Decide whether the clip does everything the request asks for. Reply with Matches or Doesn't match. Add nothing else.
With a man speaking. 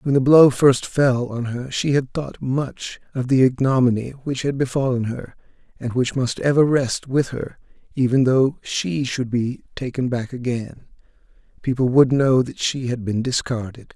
Matches